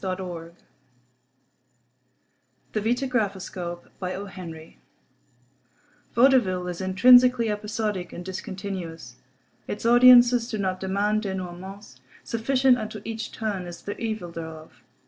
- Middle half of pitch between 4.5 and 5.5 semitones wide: No, average, 4.0 semitones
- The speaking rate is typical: No, slow, 90 wpm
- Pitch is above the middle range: Yes, high, 200 Hz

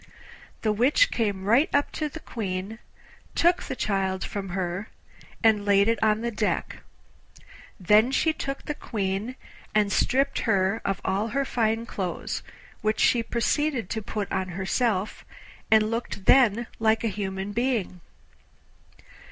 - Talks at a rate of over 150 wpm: No, average, 145 wpm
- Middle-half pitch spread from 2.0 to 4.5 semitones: Yes, average, 3.4 semitones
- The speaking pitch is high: Yes, high, 215 Hz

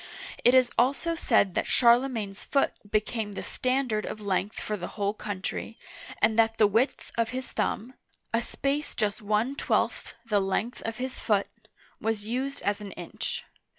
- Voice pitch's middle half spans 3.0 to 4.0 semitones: Yes, average, 3.5 semitones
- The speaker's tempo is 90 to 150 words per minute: No, average, 175 wpm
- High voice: Yes, high, 225 Hz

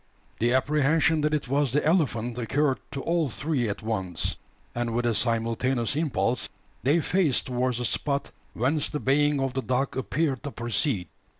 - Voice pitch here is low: Yes, low, 130 Hz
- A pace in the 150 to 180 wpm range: Yes, average, 170 wpm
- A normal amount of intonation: Yes, average, 3.9 semitones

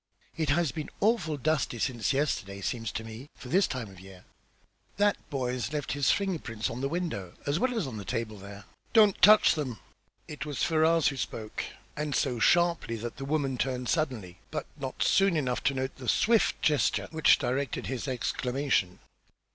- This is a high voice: No, low, 135 Hz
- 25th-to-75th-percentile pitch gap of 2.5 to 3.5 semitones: No, average, 5.2 semitones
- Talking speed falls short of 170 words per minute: No, average, 180 wpm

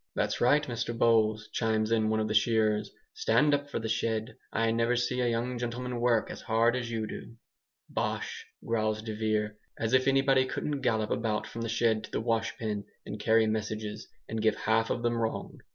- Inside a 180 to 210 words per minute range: Yes, average, 200 wpm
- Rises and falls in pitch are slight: Yes, narrow, 1.8 semitones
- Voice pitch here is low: Yes, low, 115 Hz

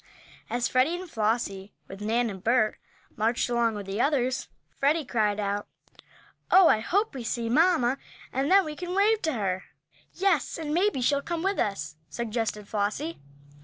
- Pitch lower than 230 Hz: No, high, 245 Hz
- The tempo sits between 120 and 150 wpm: No, average, 165 wpm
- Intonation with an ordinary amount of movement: No, wide, 7.1 semitones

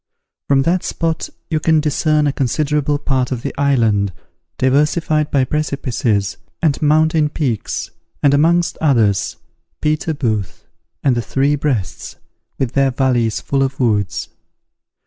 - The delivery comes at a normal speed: No, slow, 130 wpm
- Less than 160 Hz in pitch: Yes, medium, 140 Hz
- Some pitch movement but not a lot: Yes, average, 3.7 semitones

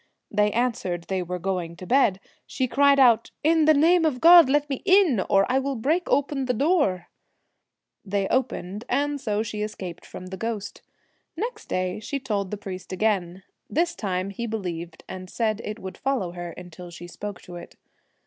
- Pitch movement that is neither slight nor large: No, wide, 6.8 semitones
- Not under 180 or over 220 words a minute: Yes, average, 195 wpm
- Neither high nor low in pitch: No, high, 215 Hz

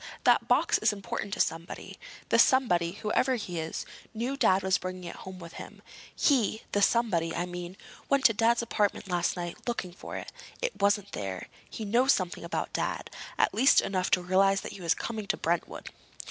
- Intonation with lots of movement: No, average, 4.4 semitones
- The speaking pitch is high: Yes, high, 195 Hz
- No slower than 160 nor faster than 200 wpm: Yes, average, 180 wpm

